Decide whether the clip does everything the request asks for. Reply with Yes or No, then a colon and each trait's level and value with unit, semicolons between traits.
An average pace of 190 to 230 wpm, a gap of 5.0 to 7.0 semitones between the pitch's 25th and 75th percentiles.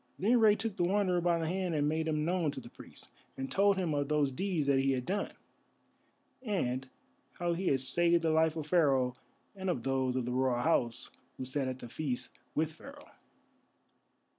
Yes: average, 200 wpm; average, 5.3 semitones